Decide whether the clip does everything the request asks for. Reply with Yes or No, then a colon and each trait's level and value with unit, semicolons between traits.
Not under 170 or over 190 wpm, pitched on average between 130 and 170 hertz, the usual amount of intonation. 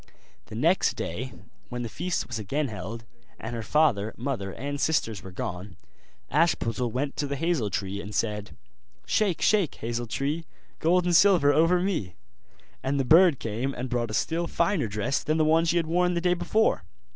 No: average, 185 wpm; medium, 140 Hz; wide, 7.0 semitones